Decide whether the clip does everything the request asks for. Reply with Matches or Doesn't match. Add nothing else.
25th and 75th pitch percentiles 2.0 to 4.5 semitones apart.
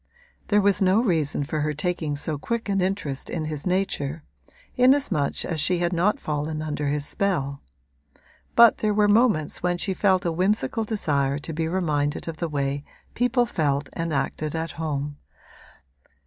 Doesn't match